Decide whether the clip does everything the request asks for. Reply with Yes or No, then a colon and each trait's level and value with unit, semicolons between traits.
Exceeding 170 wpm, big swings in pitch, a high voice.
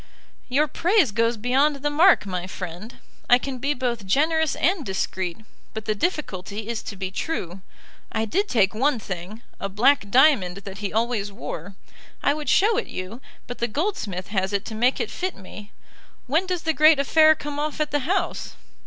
Yes: average, 190 wpm; wide, 7.2 semitones; high, 240 Hz